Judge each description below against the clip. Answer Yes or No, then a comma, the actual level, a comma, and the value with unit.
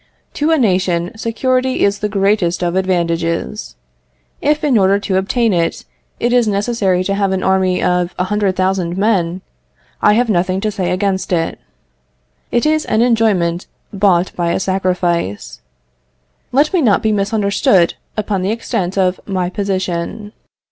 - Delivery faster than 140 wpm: Yes, average, 155 wpm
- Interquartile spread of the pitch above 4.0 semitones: No, average, 3.1 semitones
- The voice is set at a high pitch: Yes, high, 195 Hz